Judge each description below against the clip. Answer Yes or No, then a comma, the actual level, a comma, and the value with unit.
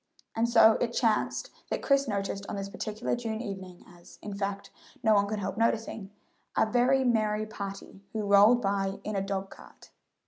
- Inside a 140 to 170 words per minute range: No, average, 180 wpm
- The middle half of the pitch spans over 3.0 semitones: No, narrow, 2.4 semitones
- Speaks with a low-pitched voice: No, high, 210 Hz